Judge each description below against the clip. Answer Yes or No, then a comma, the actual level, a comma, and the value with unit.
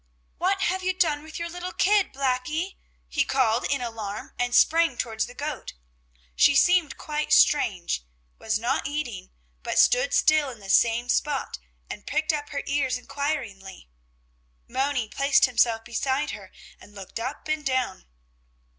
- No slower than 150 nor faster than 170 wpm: Yes, average, 155 wpm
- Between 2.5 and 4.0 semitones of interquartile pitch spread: No, average, 4.8 semitones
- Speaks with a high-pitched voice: Yes, very high, 275 Hz